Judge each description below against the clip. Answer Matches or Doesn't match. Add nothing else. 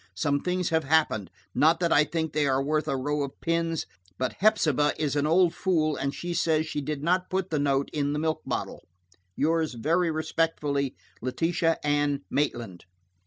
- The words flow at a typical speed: Matches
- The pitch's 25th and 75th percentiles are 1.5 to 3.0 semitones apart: Matches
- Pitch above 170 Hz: Doesn't match